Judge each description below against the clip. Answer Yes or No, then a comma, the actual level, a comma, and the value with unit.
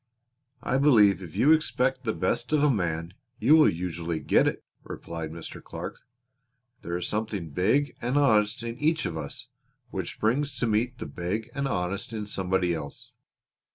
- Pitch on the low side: Yes, low, 105 Hz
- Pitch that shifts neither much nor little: No, wide, 6.7 semitones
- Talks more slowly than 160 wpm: No, average, 170 wpm